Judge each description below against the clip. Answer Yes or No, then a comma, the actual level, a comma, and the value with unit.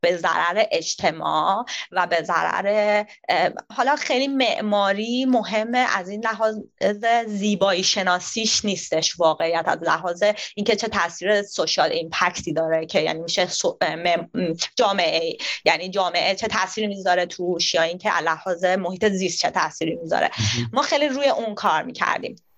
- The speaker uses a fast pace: No, average, 135 wpm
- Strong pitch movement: No, average, 3.9 semitones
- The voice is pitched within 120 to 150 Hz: No, high, 200 Hz